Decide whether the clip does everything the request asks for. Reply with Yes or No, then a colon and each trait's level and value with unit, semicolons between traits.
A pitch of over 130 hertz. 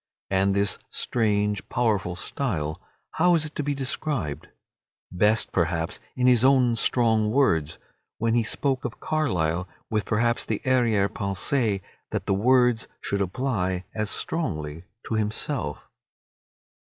No: low, 110 Hz